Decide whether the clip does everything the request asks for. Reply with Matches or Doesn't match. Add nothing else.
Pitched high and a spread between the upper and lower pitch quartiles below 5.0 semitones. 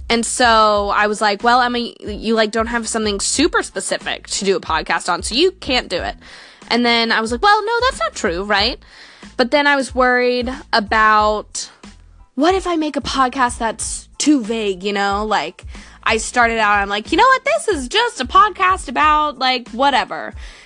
Doesn't match